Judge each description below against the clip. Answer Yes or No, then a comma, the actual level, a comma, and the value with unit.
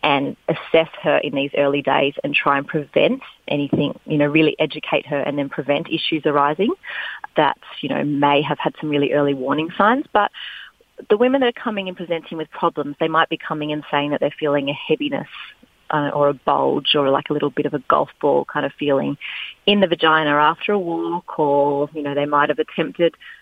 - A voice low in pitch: No, medium, 150 Hz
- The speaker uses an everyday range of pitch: No, narrow, 2.2 semitones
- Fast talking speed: Yes, fast, 215 wpm